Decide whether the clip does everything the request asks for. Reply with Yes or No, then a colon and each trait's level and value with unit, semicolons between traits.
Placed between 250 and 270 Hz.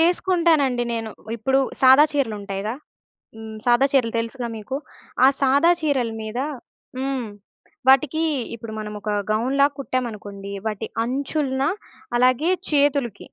Yes: very high, 255 Hz